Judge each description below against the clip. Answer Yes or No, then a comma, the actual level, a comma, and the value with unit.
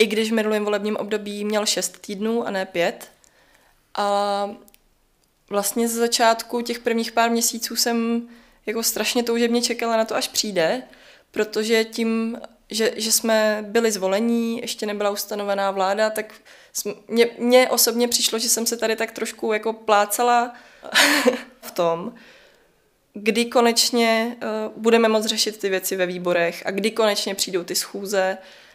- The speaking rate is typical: Yes, average, 145 wpm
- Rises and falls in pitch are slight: Yes, narrow, 2.1 semitones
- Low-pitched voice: No, high, 225 Hz